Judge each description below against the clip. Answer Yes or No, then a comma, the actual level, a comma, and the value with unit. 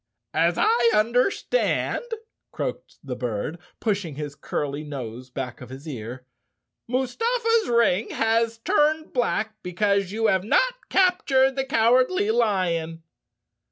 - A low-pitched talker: No, high, 215 Hz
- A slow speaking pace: Yes, slow, 125 wpm